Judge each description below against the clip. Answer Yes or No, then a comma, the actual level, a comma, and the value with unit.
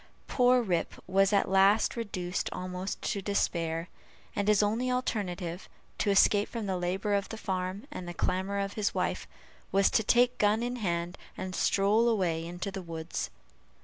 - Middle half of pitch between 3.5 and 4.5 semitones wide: No, average, 2.7 semitones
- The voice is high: Yes, high, 195 Hz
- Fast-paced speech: No, average, 170 wpm